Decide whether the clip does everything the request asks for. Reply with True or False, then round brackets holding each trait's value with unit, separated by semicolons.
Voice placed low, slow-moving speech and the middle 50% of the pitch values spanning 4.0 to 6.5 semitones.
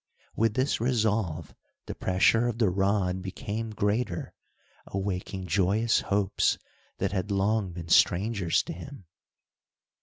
False (100 Hz; 120 wpm; 3.3 semitones)